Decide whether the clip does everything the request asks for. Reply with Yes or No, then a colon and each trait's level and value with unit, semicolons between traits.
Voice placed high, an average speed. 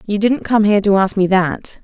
No: high, 200 Hz; fast, 260 wpm